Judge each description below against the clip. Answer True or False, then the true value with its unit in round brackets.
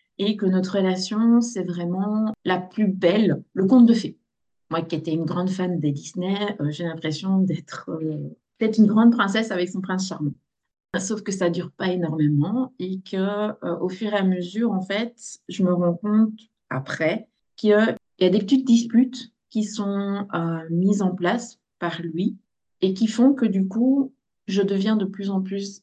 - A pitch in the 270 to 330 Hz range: False (195 Hz)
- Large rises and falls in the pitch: False (3.5 semitones)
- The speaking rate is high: False (195 wpm)